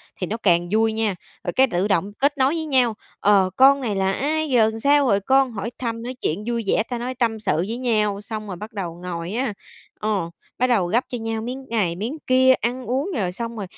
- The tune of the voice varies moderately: Yes, average, 4.3 semitones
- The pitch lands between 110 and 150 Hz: No, high, 225 Hz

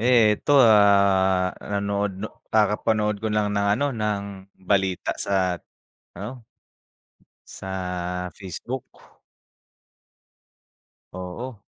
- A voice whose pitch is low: Yes, low, 100 Hz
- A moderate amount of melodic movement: No, narrow, 2.2 semitones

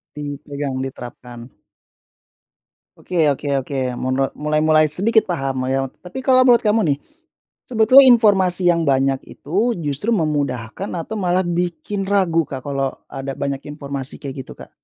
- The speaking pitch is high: No, medium, 150 Hz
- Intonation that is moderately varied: No, wide, 5.8 semitones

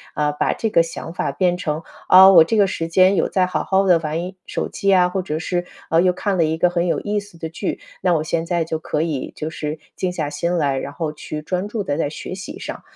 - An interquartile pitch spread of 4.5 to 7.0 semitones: No, average, 2.8 semitones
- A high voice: No, medium, 170 Hz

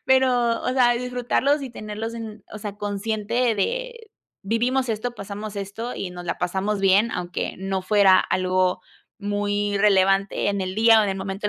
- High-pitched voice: Yes, high, 210 Hz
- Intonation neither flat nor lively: Yes, average, 3.2 semitones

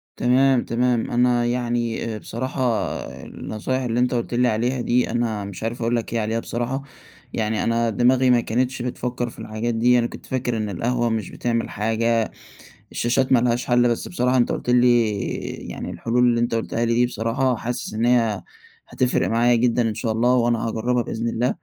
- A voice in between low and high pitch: No, low, 120 Hz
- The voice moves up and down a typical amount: No, narrow, 1.3 semitones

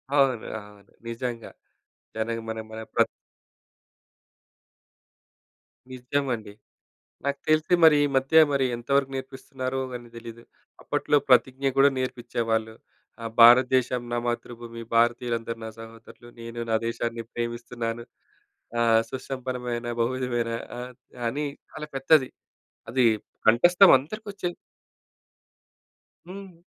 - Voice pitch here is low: Yes, low, 120 Hz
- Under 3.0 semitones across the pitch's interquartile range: Yes, narrow, 2.4 semitones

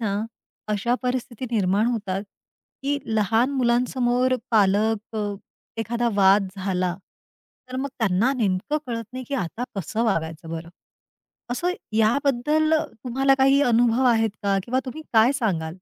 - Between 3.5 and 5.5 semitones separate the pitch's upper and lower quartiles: Yes, average, 4.2 semitones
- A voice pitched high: Yes, high, 230 Hz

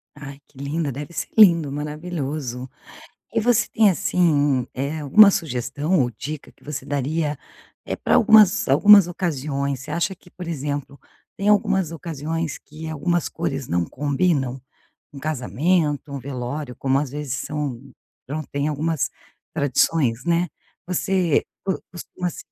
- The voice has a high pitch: No, medium, 150 Hz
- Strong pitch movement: No, average, 3.8 semitones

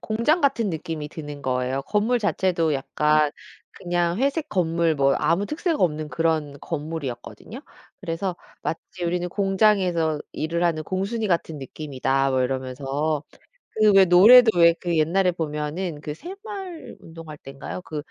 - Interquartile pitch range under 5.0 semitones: Yes, average, 4.5 semitones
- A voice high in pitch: No, medium, 165 Hz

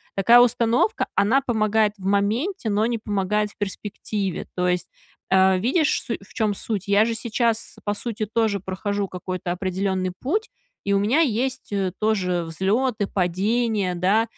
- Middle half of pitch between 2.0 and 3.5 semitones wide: Yes, average, 3.2 semitones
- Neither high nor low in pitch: No, high, 205 Hz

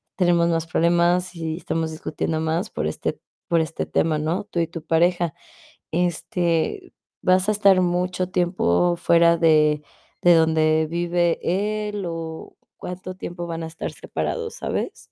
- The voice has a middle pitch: Yes, medium, 170 Hz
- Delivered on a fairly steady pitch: Yes, narrow, 1.8 semitones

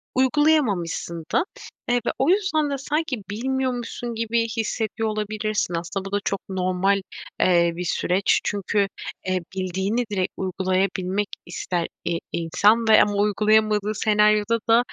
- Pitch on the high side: Yes, high, 210 Hz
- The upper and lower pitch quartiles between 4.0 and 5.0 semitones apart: No, average, 3.6 semitones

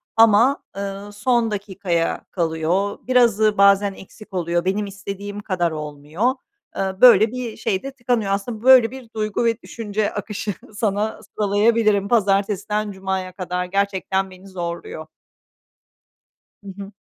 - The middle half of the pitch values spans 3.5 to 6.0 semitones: No, narrow, 2.5 semitones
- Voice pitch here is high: Yes, high, 200 Hz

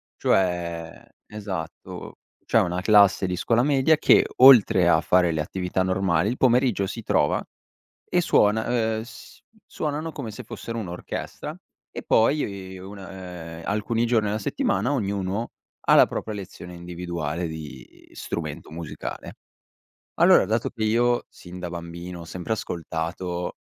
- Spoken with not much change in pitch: No, average, 4.5 semitones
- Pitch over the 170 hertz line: No, very low, 95 Hz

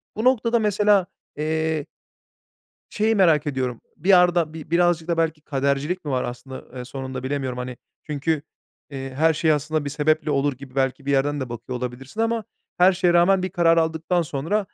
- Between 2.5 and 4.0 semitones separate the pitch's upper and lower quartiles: No, average, 4.5 semitones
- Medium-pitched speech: Yes, medium, 155 Hz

